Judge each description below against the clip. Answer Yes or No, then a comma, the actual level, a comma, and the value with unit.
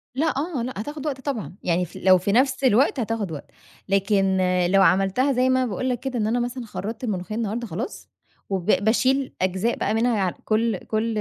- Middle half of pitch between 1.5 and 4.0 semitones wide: No, average, 4.8 semitones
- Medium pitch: No, high, 225 Hz